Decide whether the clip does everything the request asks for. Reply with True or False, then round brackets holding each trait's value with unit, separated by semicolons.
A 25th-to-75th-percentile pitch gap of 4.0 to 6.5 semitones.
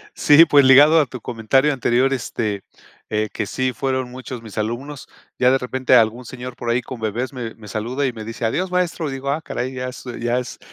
False (2.6 semitones)